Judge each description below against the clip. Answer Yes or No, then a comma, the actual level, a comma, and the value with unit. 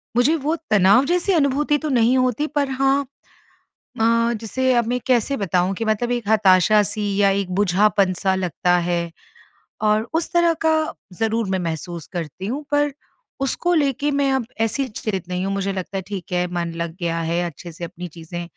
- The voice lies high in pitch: Yes, high, 210 Hz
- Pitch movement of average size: No, wide, 6.8 semitones